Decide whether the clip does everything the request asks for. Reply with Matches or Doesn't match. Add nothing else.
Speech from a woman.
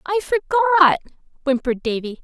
Matches